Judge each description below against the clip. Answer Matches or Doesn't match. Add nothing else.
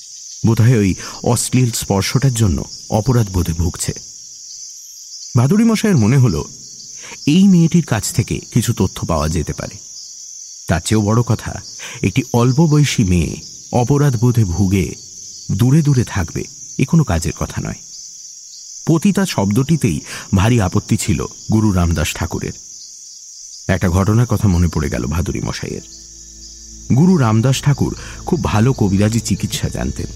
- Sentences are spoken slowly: Matches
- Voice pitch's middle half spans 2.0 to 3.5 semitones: Doesn't match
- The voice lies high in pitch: Doesn't match